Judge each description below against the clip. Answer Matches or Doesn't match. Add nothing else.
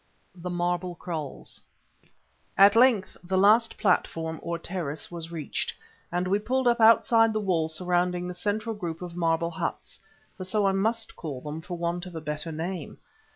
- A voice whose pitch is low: Doesn't match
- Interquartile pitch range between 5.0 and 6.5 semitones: Doesn't match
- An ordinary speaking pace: Matches